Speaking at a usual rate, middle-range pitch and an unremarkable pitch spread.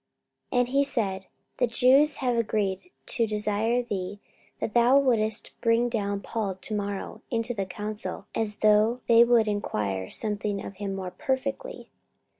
No: average, 155 wpm; high, 220 Hz; average, 3.1 semitones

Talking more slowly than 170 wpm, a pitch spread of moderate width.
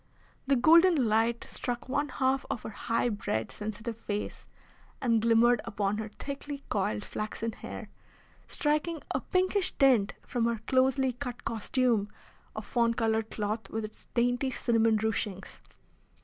Yes: average, 140 wpm; average, 3.4 semitones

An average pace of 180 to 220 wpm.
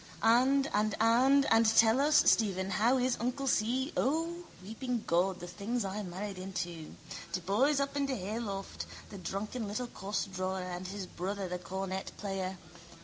No: average, 160 wpm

